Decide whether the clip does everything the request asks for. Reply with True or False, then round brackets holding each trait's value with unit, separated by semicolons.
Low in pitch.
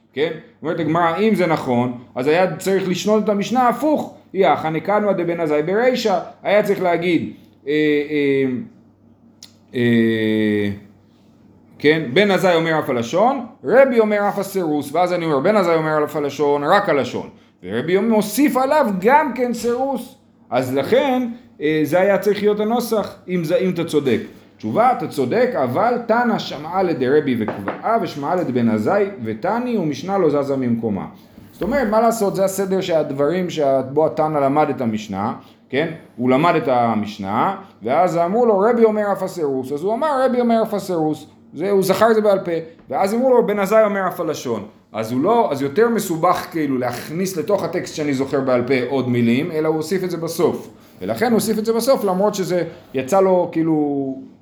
False (175 Hz)